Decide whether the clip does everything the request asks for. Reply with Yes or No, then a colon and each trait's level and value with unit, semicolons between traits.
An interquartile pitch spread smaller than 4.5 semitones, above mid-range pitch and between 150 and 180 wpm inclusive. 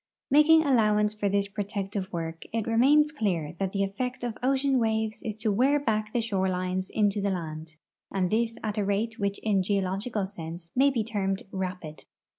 No: average, 3.2 semitones; high, 210 Hz; average, 190 wpm